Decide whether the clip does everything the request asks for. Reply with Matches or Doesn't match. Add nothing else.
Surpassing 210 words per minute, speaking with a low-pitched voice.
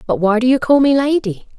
Doesn't match